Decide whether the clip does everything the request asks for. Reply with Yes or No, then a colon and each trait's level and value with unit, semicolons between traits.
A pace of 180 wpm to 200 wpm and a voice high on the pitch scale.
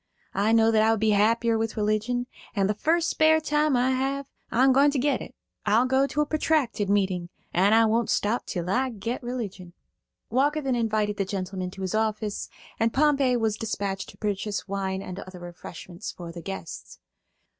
Yes: average, 190 wpm; high, 220 Hz